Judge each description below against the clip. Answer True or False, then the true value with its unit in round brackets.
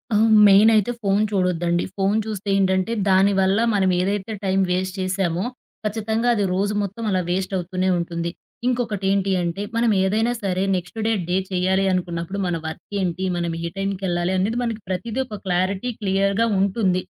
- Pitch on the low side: False (195 Hz)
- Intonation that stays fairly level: True (2.1 semitones)